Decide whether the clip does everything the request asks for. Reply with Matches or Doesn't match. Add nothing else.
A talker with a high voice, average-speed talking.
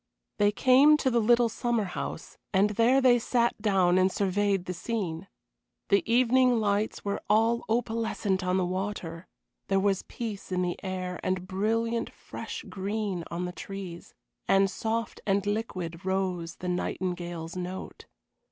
Matches